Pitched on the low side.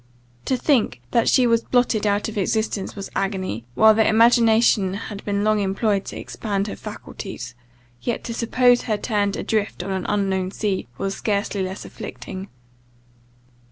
No: high, 205 Hz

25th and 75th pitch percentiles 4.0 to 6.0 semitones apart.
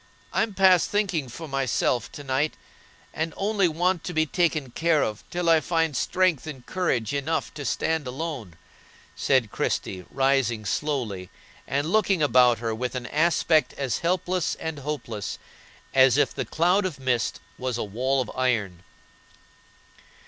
Yes: average, 5.1 semitones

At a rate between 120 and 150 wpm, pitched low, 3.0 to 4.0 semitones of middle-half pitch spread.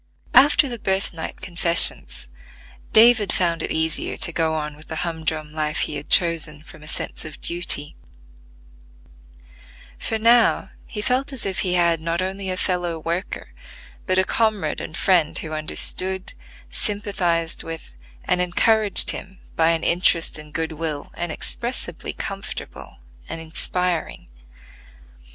No: slow, 135 wpm; medium, 170 Hz; average, 3.3 semitones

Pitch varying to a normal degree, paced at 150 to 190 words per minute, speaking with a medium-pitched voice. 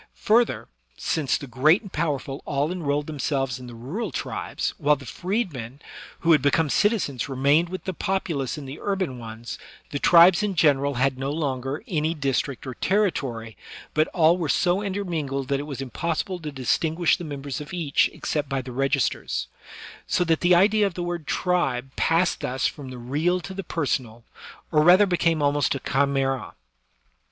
Yes: average, 4.6 semitones; average, 175 wpm; medium, 150 Hz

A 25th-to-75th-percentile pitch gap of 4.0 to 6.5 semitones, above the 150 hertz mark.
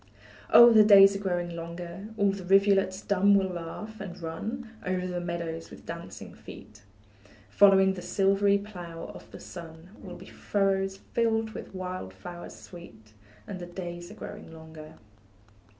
No: narrow, 2.6 semitones; medium, 185 Hz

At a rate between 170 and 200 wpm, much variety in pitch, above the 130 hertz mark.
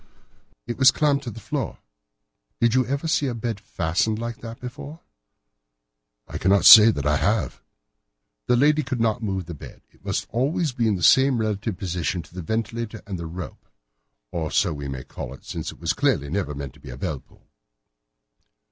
No: average, 190 wpm; wide, 7.0 semitones; low, 105 Hz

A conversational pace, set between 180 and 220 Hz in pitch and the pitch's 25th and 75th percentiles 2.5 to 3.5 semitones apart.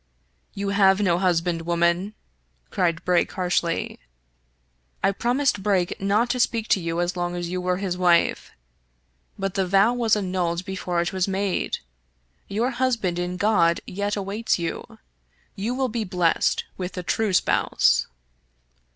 Yes: average, 160 wpm; medium, 185 Hz; average, 2.8 semitones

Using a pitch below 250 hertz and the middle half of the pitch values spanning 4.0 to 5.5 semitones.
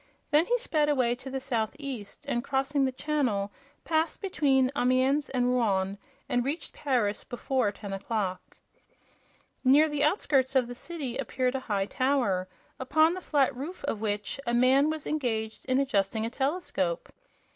No: very high, 260 Hz; average, 4.4 semitones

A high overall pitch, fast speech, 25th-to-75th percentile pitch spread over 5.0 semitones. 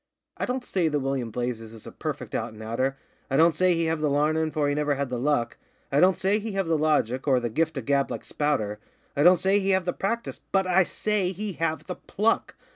No: medium, 155 Hz; fast, 250 wpm; wide, 5.4 semitones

